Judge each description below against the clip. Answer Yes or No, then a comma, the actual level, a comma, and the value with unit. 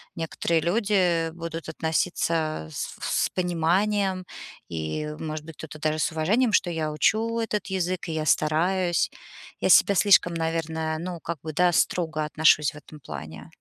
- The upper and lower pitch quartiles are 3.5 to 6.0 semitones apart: No, average, 2.8 semitones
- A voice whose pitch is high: No, medium, 165 Hz